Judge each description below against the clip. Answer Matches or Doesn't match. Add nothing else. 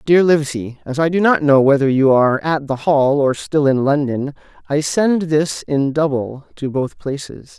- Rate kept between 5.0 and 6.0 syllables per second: Doesn't match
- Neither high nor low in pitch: Matches